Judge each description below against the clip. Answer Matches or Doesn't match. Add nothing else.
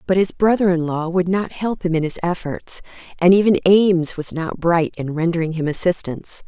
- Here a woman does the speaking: Matches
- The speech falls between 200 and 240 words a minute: Matches